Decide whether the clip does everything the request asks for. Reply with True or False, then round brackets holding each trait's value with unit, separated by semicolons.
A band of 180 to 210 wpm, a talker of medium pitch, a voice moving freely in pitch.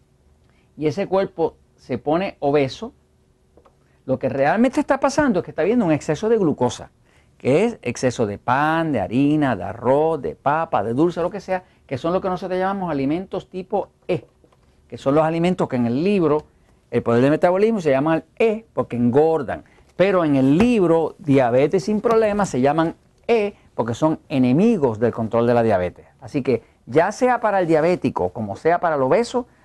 True (185 wpm; 160 Hz; 6.9 semitones)